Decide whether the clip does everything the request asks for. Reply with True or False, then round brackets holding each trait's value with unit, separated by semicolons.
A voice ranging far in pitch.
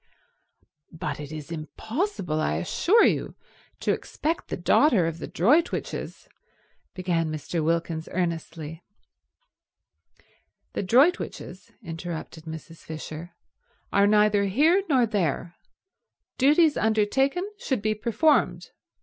True (8.2 semitones)